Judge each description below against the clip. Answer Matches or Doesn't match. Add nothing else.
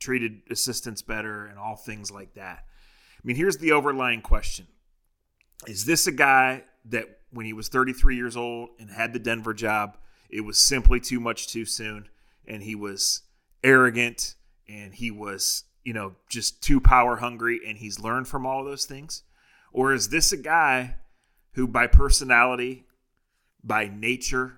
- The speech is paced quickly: Doesn't match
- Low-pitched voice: Matches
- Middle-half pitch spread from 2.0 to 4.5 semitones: Matches